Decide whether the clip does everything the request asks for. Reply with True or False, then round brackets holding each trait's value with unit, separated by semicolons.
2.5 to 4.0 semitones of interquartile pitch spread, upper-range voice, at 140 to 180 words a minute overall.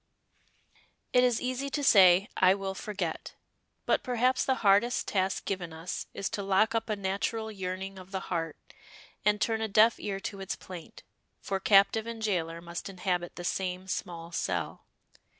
True (3.3 semitones; 195 Hz; 170 wpm)